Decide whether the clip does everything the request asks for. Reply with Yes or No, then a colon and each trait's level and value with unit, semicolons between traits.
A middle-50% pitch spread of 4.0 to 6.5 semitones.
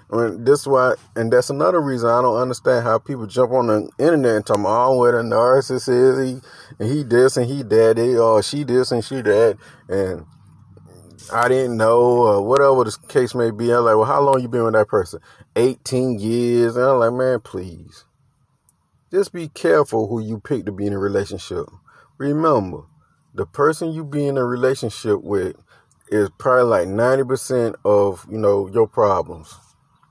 No: average, 3.0 semitones